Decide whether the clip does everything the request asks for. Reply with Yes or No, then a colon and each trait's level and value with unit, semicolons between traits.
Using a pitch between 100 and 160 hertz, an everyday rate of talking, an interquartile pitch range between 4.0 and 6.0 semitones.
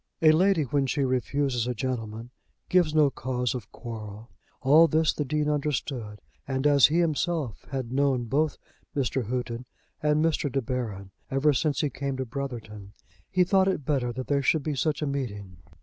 No: low, 135 Hz; average, 180 wpm; average, 3.6 semitones